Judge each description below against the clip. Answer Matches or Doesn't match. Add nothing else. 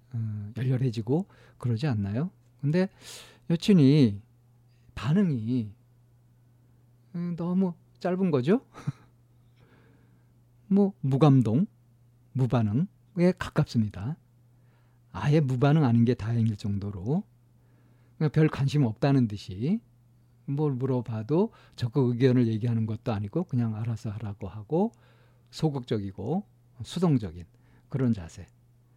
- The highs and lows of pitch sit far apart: Doesn't match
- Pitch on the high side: Doesn't match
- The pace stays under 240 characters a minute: Matches